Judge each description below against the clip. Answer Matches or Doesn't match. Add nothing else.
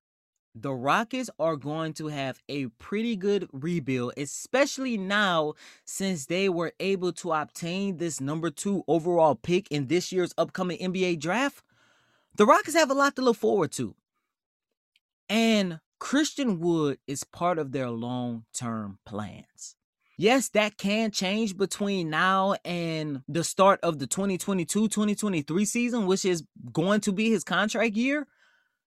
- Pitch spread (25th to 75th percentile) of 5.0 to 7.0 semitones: Matches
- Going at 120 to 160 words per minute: Matches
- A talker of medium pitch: Matches